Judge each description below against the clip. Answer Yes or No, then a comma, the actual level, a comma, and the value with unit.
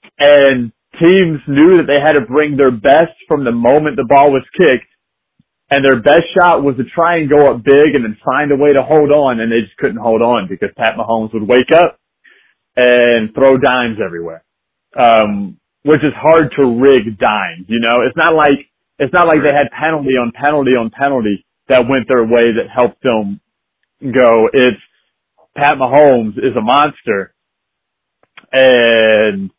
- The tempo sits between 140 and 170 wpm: No, average, 180 wpm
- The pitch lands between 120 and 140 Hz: Yes, low, 135 Hz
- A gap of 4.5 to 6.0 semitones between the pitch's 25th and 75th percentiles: No, average, 4.1 semitones